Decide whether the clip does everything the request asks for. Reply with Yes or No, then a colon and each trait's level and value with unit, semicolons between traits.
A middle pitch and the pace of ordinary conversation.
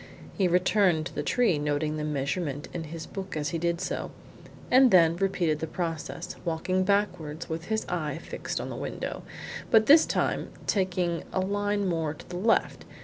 Yes: medium, 170 Hz; average, 180 wpm